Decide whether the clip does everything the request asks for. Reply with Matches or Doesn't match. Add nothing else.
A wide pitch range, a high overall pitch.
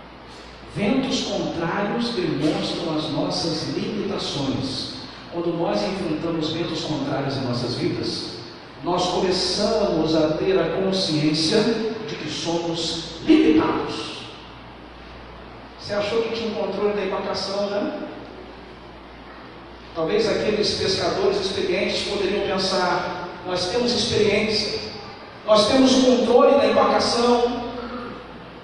Doesn't match